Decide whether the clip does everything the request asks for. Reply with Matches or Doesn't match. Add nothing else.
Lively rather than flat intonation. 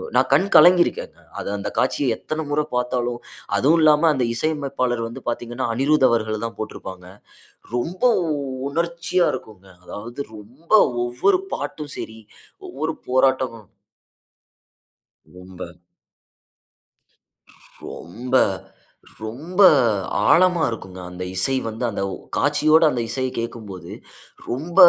Matches